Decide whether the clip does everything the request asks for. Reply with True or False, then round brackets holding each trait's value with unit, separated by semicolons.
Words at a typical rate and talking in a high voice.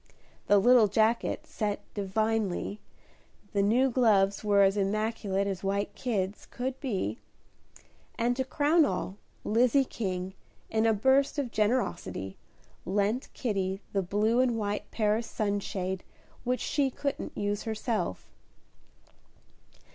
False (120 wpm; 215 Hz)